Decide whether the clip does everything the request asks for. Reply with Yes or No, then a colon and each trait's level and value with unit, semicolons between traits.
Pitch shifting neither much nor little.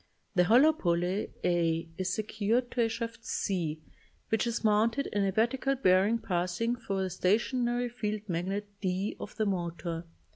Yes: average, 4.4 semitones